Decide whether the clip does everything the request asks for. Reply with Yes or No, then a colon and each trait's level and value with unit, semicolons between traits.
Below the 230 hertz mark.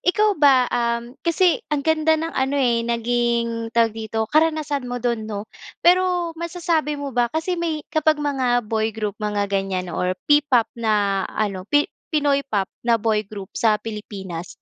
No: high, 240 Hz